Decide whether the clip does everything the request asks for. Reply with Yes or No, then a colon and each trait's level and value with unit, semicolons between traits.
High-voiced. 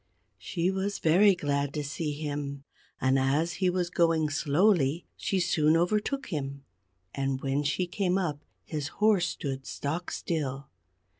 No: medium, 155 Hz